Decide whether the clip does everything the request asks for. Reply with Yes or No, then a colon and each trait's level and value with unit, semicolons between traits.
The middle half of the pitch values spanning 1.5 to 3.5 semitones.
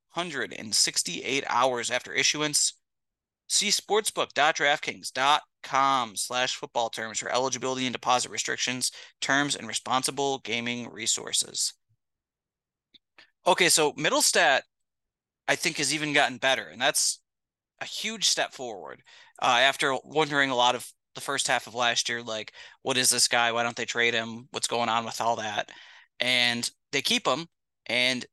Yes: average, 2.9 semitones